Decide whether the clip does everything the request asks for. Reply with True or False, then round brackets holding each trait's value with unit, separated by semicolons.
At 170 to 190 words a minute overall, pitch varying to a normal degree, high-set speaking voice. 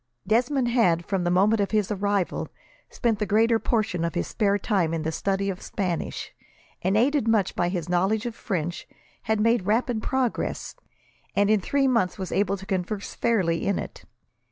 True (180 wpm; 3.7 semitones; 200 Hz)